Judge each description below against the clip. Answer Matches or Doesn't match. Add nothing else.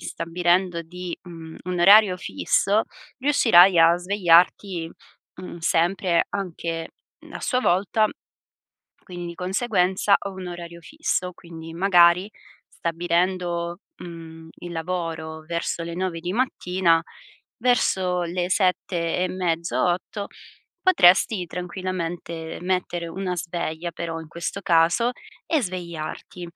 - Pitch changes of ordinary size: Doesn't match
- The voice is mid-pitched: Matches